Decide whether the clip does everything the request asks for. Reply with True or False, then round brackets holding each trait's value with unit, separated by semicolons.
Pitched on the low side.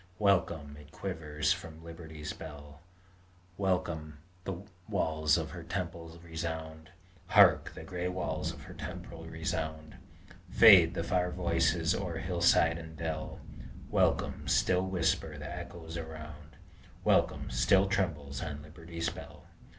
True (80 Hz)